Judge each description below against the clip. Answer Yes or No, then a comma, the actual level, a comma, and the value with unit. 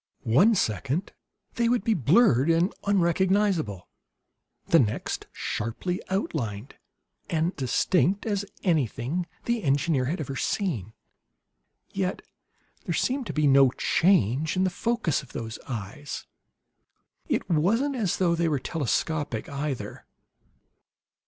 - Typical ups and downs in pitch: No, wide, 6.1 semitones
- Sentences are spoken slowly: Yes, slow, 120 wpm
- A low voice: No, medium, 165 Hz